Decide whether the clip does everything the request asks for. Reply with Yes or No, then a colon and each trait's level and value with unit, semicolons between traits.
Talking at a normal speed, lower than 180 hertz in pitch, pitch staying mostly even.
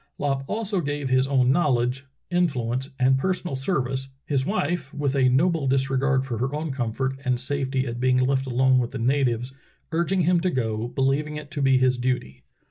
Yes: average, 185 wpm; low, 135 Hz; narrow, 2.2 semitones